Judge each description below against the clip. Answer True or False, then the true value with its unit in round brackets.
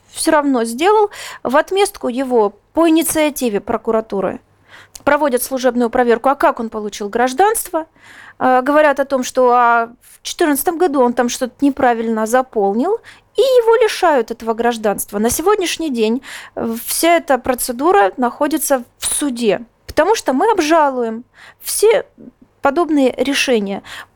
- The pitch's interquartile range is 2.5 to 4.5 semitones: False (5.4 semitones)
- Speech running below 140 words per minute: True (130 wpm)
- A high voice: True (260 Hz)